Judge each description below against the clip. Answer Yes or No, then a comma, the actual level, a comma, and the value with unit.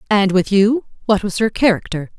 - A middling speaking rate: Yes, average, 190 wpm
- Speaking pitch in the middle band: No, high, 205 Hz